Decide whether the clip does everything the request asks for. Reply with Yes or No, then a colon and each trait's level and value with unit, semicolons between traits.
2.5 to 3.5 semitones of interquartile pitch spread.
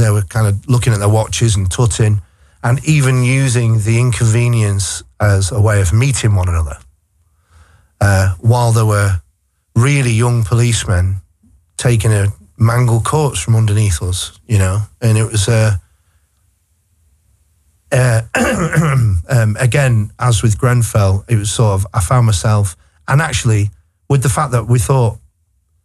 No: average, 4.6 semitones